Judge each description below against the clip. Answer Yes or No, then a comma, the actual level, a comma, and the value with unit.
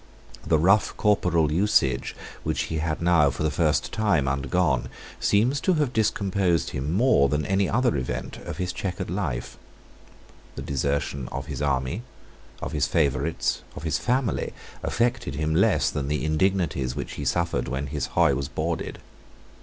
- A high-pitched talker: No, very low, 80 Hz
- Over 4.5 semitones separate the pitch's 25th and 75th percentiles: Yes, wide, 5.6 semitones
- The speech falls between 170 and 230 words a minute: No, average, 160 wpm